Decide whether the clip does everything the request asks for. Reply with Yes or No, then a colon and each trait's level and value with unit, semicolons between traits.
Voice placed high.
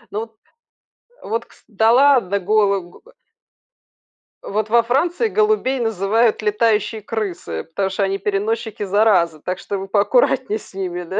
Yes: high, 210 Hz